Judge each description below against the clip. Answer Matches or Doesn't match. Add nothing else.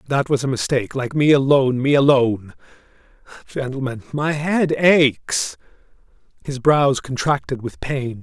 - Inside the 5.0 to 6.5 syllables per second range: Doesn't match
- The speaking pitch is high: Doesn't match